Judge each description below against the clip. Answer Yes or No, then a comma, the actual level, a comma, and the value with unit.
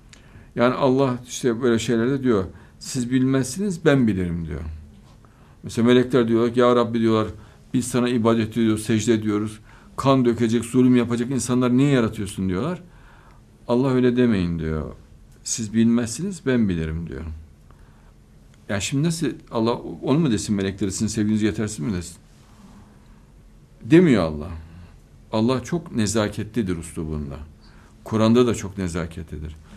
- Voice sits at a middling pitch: No, low, 110 Hz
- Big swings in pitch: Yes, wide, 5.7 semitones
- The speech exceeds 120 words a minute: Yes, average, 130 wpm